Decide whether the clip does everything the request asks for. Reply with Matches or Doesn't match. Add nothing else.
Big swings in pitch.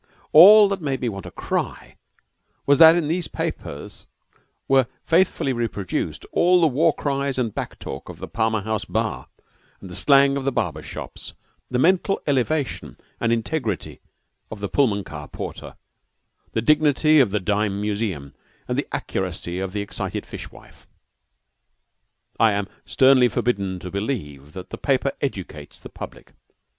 Matches